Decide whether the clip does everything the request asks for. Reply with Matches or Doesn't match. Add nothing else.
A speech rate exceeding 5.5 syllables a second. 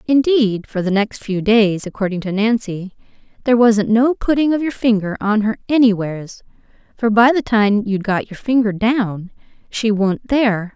Doesn't match